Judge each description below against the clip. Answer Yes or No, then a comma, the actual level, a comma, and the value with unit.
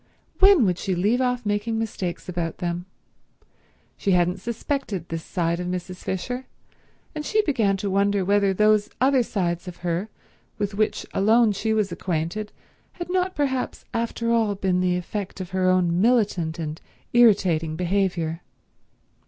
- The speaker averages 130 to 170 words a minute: Yes, average, 150 wpm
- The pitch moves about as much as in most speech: Yes, average, 4.3 semitones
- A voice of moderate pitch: No, high, 195 Hz